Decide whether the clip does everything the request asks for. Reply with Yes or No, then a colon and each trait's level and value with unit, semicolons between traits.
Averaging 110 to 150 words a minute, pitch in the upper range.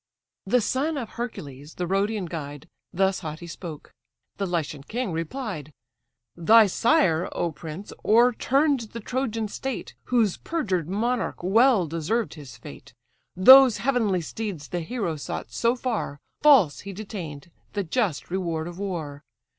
Yes: average, 140 wpm; high, 195 Hz